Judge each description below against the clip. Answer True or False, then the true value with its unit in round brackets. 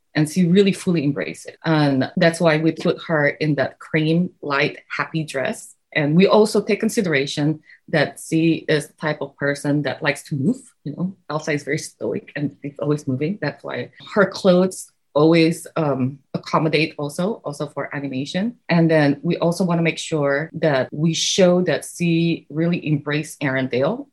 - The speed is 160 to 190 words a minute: True (175 wpm)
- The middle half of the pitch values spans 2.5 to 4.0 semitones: True (2.9 semitones)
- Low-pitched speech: False (155 Hz)